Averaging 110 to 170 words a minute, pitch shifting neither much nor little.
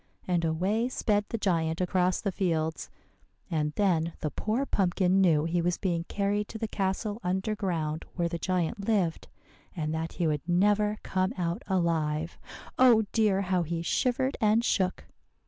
Yes: average, 165 wpm; average, 3.8 semitones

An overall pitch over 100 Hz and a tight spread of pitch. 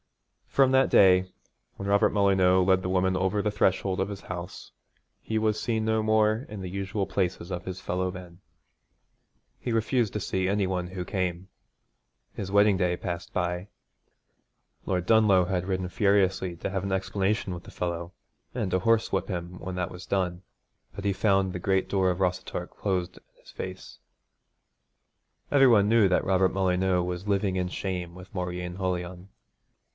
No: very low, 95 Hz; narrow, 1.9 semitones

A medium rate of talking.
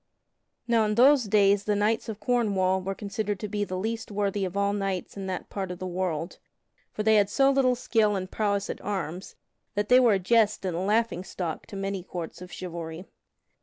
No: fast, 210 wpm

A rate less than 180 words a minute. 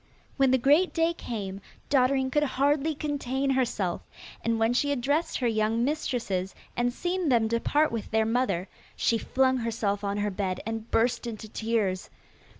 Yes: average, 165 wpm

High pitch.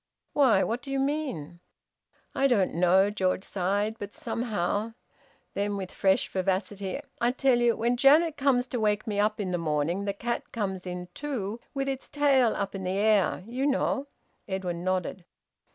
Yes: high, 205 Hz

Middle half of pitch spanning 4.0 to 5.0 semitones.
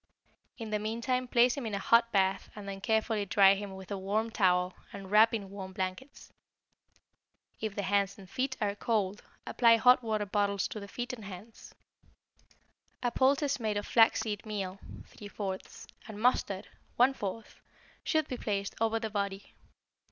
No: average, 2.7 semitones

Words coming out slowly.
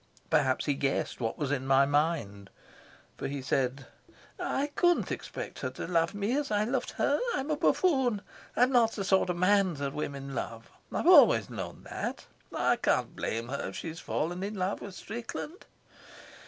No: average, 180 wpm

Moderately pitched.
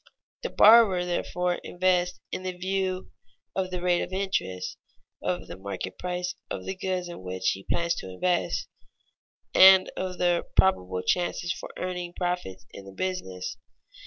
Yes: medium, 180 Hz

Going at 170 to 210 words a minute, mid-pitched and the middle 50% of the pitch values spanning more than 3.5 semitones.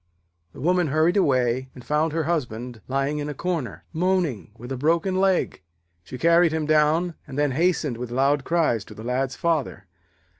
Yes: average, 180 wpm; medium, 150 Hz; average, 4.6 semitones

